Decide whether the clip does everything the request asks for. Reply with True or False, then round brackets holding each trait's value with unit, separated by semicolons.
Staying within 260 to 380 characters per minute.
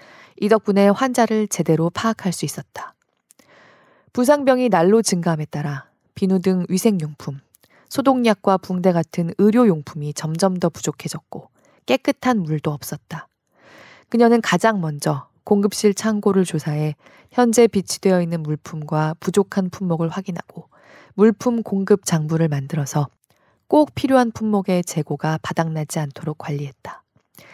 True (290 characters per minute)